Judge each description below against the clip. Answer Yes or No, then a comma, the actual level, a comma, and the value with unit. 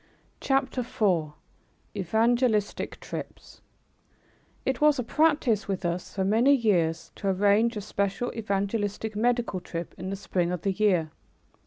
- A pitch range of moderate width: Yes, average, 4.1 semitones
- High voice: Yes, high, 205 Hz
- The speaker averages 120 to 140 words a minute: Yes, slow, 135 wpm